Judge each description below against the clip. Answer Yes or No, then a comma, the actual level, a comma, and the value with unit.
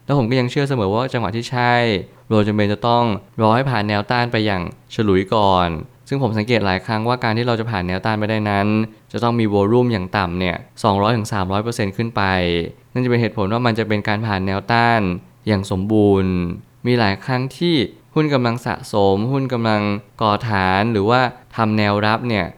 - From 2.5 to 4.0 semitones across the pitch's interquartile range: Yes, average, 3.4 semitones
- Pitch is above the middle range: No, low, 110 Hz